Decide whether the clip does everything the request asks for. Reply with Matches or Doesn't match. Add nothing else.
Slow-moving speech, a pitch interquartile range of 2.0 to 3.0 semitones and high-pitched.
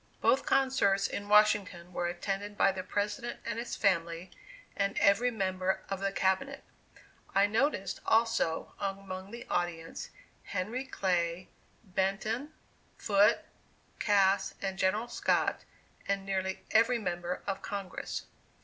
Matches